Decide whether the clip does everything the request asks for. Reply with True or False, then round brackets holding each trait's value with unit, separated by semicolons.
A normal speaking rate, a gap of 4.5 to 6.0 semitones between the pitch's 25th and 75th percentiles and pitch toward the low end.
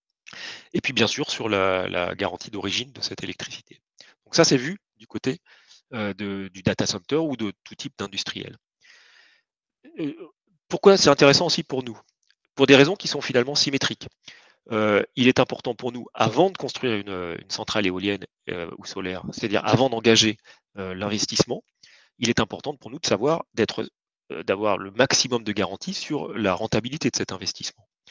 True (175 wpm; 5.5 semitones; 125 Hz)